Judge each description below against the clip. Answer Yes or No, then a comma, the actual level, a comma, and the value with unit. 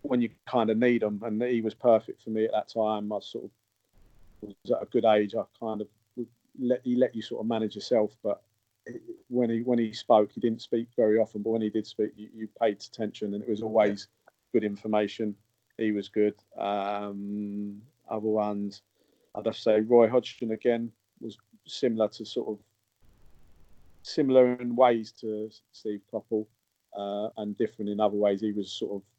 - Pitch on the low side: Yes, low, 110 Hz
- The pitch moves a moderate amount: No, narrow, 1.9 semitones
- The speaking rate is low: No, average, 195 wpm